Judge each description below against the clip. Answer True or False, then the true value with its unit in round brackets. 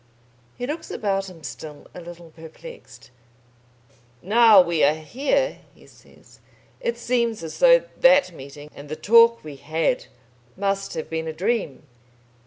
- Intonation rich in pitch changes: True (7.0 semitones)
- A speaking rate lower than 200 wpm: True (145 wpm)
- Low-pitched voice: False (185 Hz)